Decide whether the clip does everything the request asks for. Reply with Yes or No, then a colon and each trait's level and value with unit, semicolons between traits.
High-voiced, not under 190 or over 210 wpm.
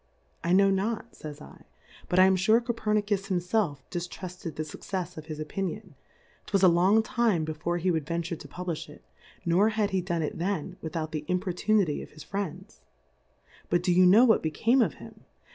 No: medium, 180 Hz; average, 195 wpm